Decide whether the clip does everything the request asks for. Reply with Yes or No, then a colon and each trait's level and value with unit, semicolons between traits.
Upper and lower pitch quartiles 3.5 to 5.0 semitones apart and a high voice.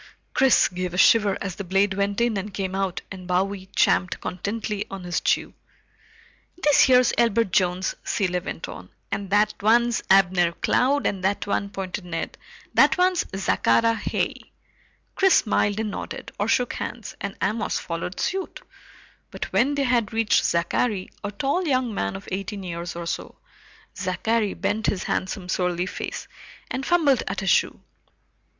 Yes: average, 3.9 semitones; high, 200 Hz